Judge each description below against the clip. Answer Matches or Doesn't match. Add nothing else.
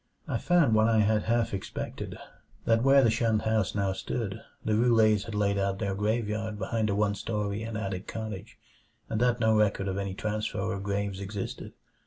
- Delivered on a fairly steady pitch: Matches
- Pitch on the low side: Matches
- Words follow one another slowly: Doesn't match